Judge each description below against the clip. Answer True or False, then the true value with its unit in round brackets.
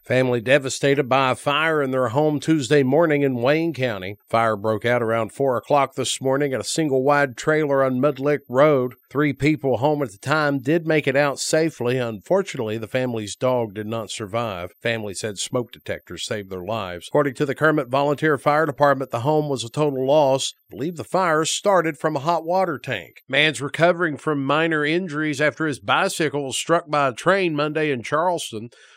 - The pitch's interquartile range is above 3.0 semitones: True (3.6 semitones)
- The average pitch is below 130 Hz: False (140 Hz)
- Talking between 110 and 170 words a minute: False (195 wpm)